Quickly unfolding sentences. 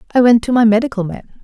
Yes: fast, 250 wpm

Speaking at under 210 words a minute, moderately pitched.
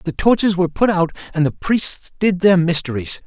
Yes: average, 200 wpm; medium, 175 Hz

